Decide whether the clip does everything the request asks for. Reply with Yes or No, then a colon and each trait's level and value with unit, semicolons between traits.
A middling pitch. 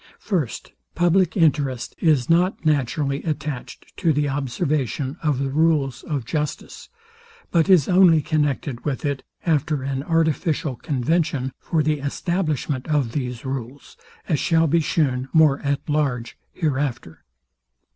Yes: medium, 145 Hz